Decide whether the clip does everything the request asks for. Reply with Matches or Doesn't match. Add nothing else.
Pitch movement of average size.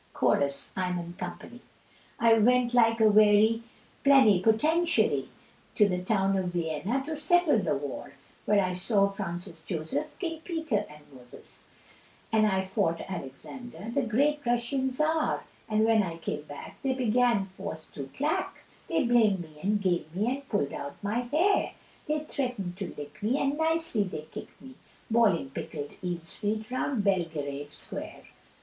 Doesn't match